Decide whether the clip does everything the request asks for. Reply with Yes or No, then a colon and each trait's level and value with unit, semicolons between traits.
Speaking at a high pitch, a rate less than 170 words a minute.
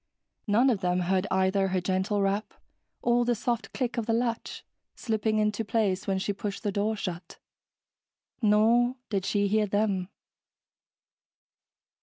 Yes: high, 205 Hz; average, 145 wpm